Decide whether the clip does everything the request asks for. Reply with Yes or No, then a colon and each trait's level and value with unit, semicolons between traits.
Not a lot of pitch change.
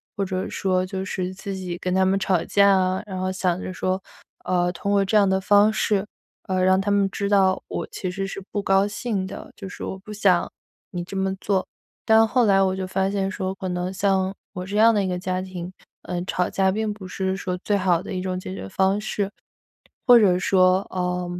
Yes: narrow, 1.4 semitones